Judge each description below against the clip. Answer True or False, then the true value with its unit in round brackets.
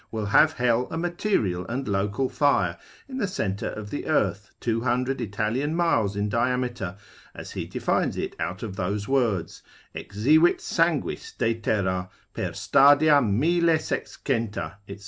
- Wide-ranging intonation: True (5.9 semitones)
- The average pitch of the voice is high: False (115 Hz)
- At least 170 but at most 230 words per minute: False (140 wpm)